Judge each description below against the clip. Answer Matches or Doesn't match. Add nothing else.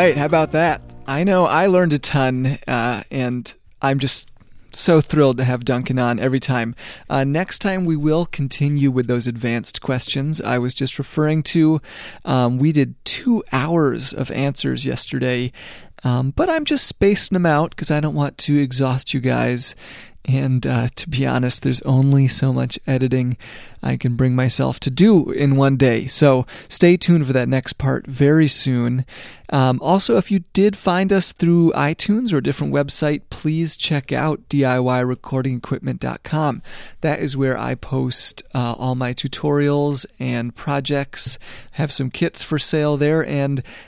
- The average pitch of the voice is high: Doesn't match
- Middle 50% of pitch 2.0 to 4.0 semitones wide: Matches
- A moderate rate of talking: Matches